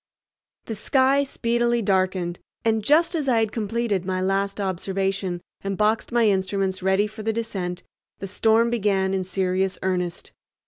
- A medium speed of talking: Yes, average, 150 wpm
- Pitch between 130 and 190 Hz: No, high, 200 Hz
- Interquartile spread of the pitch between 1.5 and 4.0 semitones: Yes, average, 3.2 semitones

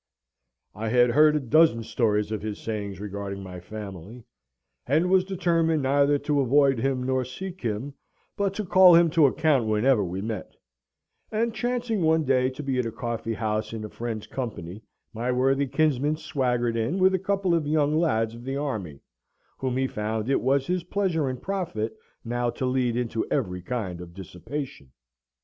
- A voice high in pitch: No, low, 130 Hz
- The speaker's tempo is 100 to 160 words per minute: No, average, 180 wpm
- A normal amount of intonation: No, wide, 5.9 semitones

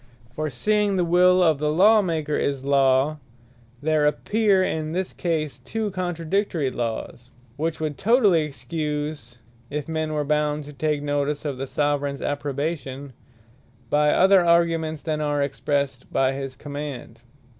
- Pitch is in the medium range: Yes, medium, 150 Hz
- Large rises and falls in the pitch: No, average, 3.0 semitones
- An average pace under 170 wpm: Yes, average, 145 wpm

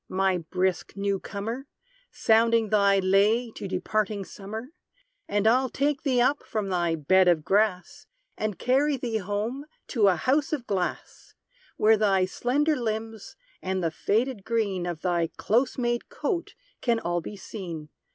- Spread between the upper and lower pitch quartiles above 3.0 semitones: Yes, average, 4.2 semitones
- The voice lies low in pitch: No, high, 210 Hz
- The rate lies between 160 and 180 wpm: No, average, 150 wpm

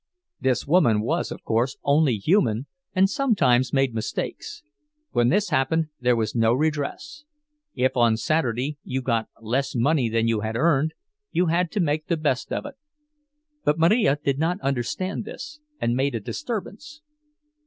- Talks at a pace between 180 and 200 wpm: No, average, 155 wpm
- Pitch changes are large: Yes, wide, 7.1 semitones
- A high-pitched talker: No, medium, 140 Hz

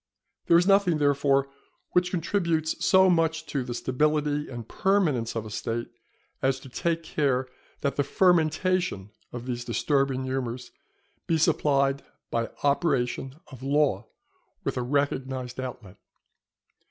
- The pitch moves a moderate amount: Yes, average, 4.2 semitones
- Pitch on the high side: No, medium, 140 Hz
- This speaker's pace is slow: Yes, slow, 130 wpm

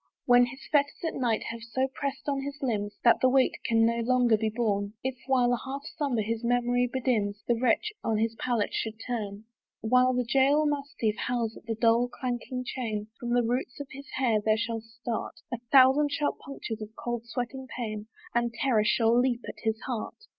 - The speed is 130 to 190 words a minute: No, average, 200 wpm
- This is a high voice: Yes, high, 240 Hz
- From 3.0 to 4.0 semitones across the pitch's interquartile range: No, narrow, 2.6 semitones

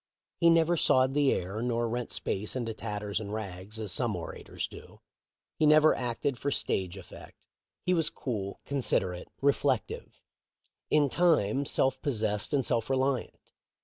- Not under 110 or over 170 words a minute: Yes, average, 155 wpm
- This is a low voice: Yes, low, 120 Hz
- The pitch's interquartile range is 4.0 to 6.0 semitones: Yes, average, 5.3 semitones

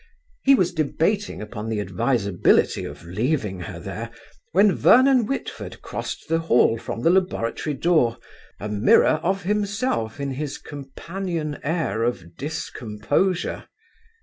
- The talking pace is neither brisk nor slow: No, slow, 125 wpm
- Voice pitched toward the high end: No, medium, 145 Hz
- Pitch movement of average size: No, wide, 8.5 semitones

